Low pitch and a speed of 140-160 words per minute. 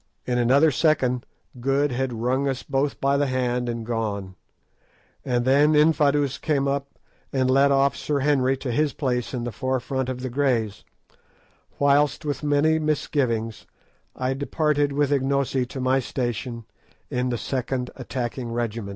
Yes: low, 130 Hz; average, 150 wpm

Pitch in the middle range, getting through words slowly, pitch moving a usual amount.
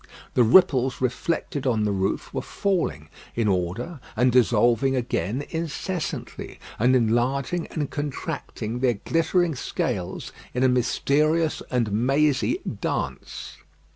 No: low, 130 Hz; slow, 115 wpm; average, 4.8 semitones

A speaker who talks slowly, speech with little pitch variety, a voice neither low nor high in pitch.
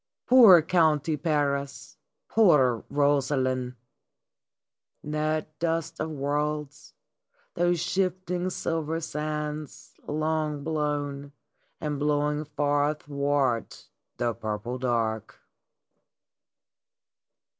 Yes: slow, 75 wpm; narrow, 2.0 semitones; medium, 150 Hz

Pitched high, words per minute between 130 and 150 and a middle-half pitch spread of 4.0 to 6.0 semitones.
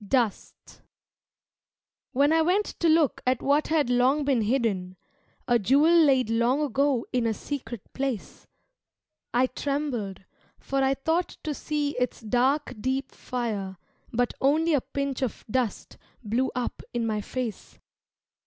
No: very high, 260 Hz; average, 140 wpm; average, 3.5 semitones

